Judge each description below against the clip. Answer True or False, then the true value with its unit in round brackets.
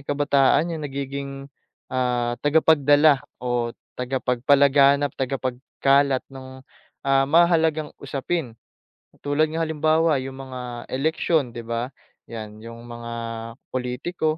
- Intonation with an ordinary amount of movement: True (3.0 semitones)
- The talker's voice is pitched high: False (135 Hz)